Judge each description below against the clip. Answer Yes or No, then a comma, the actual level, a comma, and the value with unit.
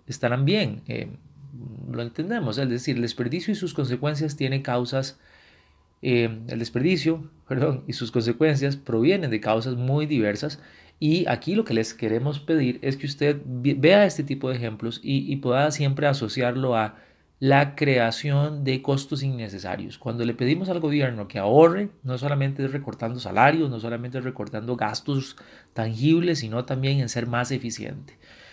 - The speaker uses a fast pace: No, average, 155 wpm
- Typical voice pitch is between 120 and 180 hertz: Yes, low, 135 Hz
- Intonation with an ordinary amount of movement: Yes, average, 3.7 semitones